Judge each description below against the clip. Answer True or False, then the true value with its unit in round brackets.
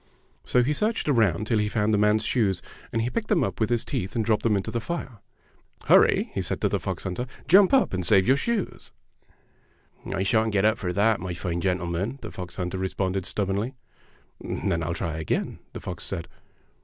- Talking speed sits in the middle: False (215 wpm)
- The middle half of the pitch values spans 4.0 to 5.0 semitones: True (4.4 semitones)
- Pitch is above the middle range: False (105 Hz)